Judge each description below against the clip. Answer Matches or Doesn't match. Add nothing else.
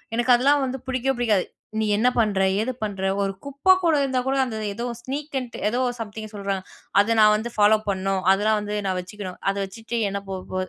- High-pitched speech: Matches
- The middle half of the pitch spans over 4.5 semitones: Doesn't match